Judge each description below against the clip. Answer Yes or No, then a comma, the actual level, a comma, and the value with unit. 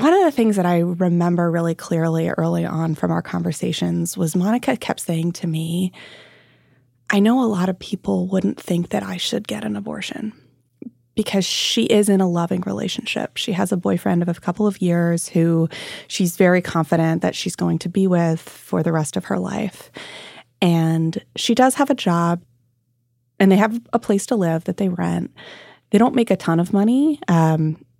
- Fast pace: No, average, 195 wpm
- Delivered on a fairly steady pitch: No, average, 3.7 semitones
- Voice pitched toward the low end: No, medium, 175 Hz